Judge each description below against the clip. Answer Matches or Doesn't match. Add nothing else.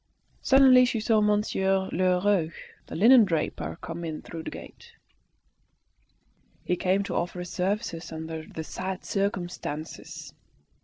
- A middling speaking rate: Doesn't match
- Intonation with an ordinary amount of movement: Matches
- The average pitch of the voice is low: Doesn't match